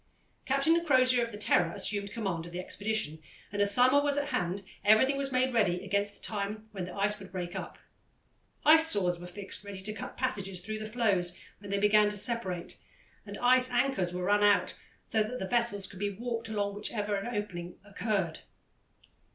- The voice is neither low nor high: No, high, 205 Hz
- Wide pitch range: No, average, 3.7 semitones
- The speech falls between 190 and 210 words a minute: Yes, average, 195 wpm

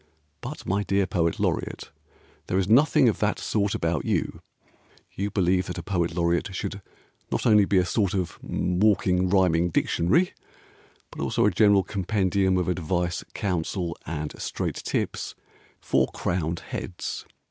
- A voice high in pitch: No, very low, 95 Hz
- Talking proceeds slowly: No, average, 145 wpm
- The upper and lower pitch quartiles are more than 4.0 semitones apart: No, narrow, 2.5 semitones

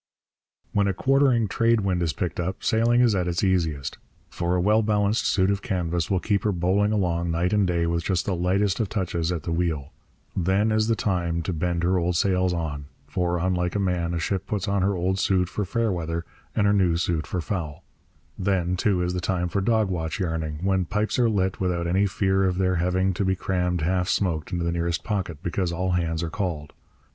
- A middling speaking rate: No, fast, 220 wpm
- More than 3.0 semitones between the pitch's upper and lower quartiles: No, narrow, 2.6 semitones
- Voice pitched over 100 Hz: No, very low, 90 Hz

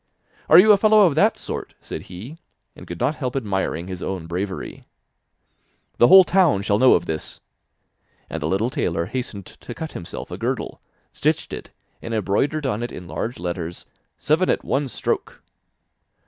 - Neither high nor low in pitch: No, low, 115 Hz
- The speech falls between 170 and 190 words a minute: Yes, average, 175 wpm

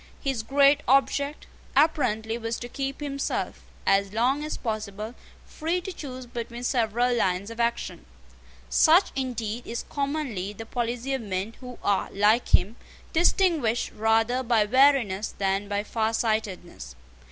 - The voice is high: Yes, high, 235 Hz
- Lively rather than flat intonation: No, average, 4.1 semitones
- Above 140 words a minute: No, slow, 135 wpm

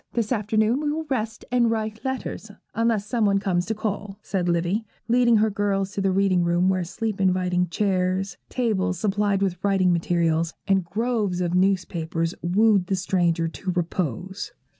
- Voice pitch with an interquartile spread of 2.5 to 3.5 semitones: Yes, average, 3.2 semitones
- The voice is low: No, high, 195 Hz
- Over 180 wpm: No, average, 165 wpm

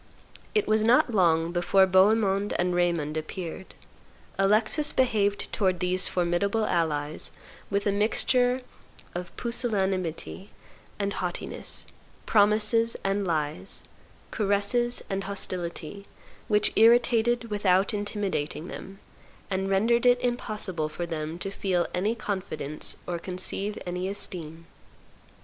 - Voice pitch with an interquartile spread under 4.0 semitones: Yes, average, 3.5 semitones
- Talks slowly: Yes, slow, 110 wpm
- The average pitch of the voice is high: Yes, high, 195 Hz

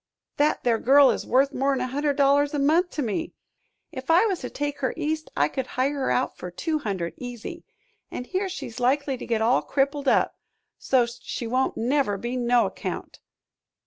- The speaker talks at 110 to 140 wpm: No, average, 195 wpm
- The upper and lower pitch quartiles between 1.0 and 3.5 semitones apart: Yes, average, 3.0 semitones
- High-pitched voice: Yes, very high, 270 Hz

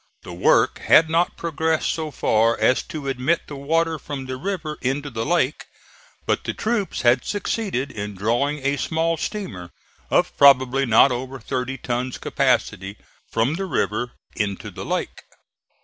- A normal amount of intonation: Yes, average, 4.9 semitones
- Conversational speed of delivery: Yes, average, 155 wpm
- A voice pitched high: No, low, 135 Hz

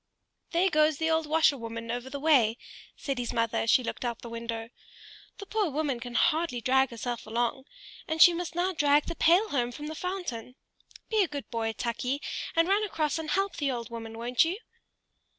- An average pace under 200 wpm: No, fast, 205 wpm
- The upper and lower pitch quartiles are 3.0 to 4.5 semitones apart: No, wide, 5.6 semitones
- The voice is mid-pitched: No, very high, 280 Hz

